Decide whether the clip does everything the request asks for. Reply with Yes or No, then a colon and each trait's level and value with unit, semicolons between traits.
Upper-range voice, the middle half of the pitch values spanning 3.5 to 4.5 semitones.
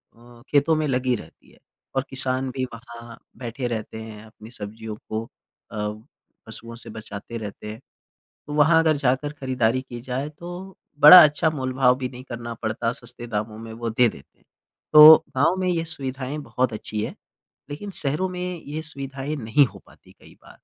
No: low, 125 Hz; average, 4.1 semitones